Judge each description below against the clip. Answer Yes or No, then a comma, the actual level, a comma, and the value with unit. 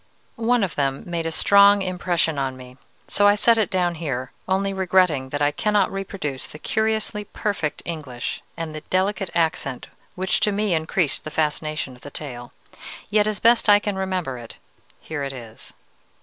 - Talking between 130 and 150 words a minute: No, average, 180 wpm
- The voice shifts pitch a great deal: Yes, wide, 5.7 semitones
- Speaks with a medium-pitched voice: Yes, medium, 175 Hz